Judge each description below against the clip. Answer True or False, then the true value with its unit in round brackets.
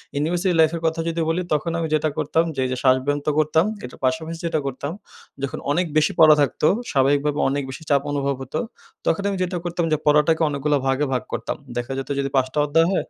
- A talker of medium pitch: True (150 Hz)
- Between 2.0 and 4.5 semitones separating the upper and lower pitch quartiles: True (2.8 semitones)